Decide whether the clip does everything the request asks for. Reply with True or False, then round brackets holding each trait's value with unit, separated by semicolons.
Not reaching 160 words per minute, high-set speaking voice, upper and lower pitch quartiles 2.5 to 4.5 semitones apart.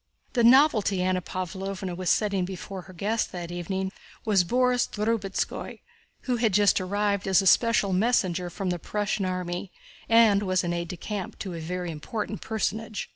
False (165 wpm; 195 Hz; 2.8 semitones)